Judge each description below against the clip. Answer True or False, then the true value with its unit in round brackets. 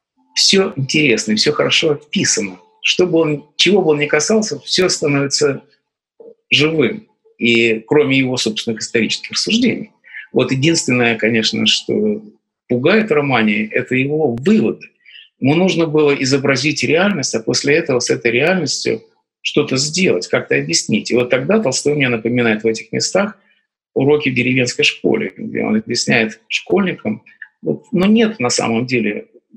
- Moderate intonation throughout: False (6.0 semitones)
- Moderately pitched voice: True (145 Hz)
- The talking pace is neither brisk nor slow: True (135 wpm)